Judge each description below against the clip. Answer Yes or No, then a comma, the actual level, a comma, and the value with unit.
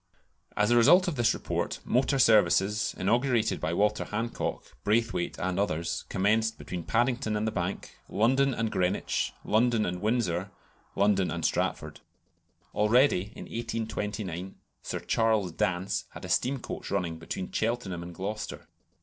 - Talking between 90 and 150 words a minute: Yes, average, 140 wpm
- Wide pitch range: No, average, 3.9 semitones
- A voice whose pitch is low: Yes, low, 105 Hz